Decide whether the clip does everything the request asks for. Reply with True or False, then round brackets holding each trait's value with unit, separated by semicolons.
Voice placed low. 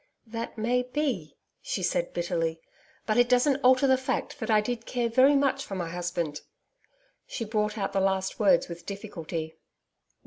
False (215 Hz)